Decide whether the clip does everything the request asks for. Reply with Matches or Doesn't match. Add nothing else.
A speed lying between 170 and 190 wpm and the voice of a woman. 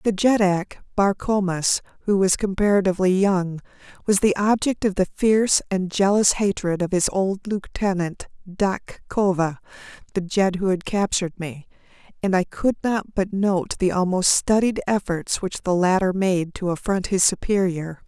Doesn't match